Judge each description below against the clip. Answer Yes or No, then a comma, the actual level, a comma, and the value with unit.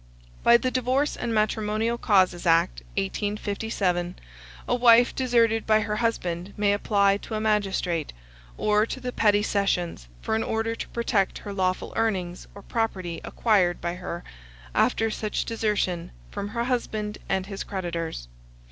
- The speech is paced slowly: No, average, 145 wpm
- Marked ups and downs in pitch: No, average, 3.5 semitones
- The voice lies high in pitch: Yes, high, 210 Hz